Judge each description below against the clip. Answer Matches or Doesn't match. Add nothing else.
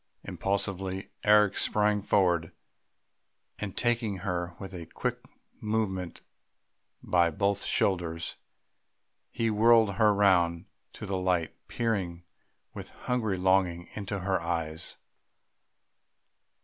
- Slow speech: Matches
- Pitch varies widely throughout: Doesn't match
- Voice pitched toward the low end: Matches